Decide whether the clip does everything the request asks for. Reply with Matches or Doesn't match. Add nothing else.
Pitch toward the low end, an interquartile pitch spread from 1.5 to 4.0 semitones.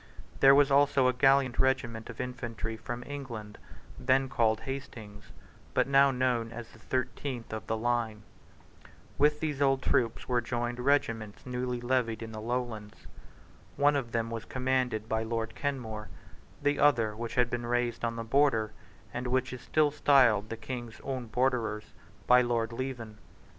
Matches